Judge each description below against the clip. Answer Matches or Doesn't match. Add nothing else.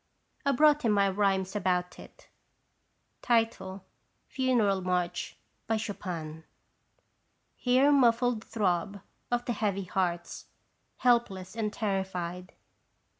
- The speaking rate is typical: Doesn't match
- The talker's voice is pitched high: Matches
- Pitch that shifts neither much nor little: Matches